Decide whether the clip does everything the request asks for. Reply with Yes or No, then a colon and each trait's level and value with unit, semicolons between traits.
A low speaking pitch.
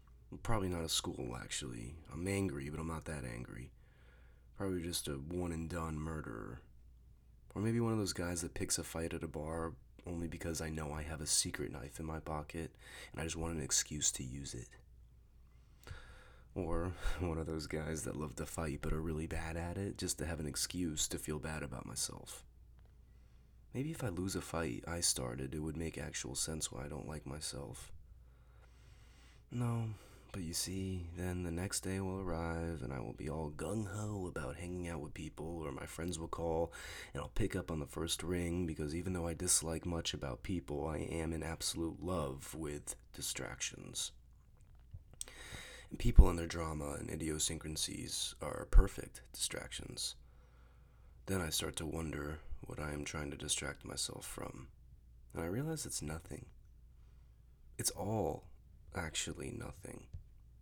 Yes: very low, 80 Hz